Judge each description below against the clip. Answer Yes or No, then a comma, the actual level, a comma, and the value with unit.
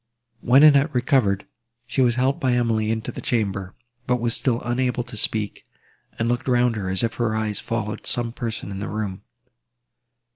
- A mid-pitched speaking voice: No, low, 115 Hz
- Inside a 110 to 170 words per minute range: No, average, 180 wpm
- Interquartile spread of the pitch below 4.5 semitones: Yes, narrow, 2.5 semitones